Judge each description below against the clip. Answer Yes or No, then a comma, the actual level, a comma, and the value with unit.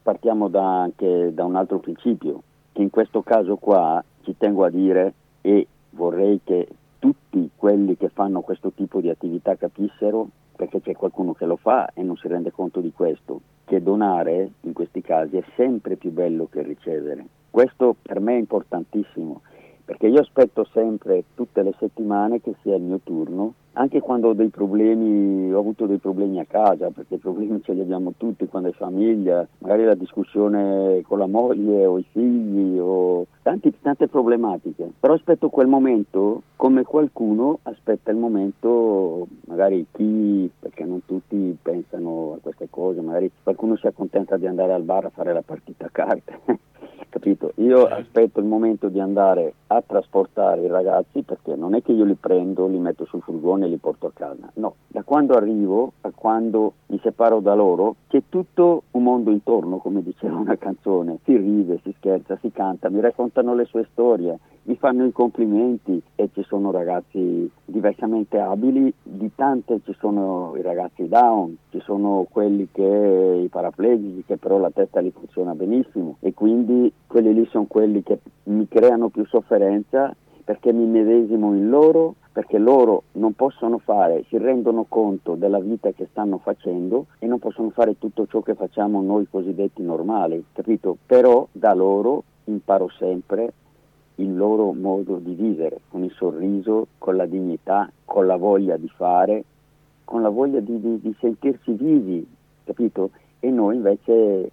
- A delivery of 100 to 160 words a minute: No, fast, 170 wpm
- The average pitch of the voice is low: Yes, low, 105 Hz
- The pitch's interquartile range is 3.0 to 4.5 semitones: Yes, average, 3.3 semitones